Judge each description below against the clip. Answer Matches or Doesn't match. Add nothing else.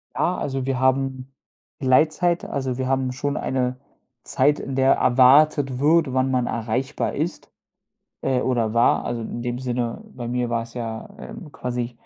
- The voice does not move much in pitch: Matches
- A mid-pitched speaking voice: Doesn't match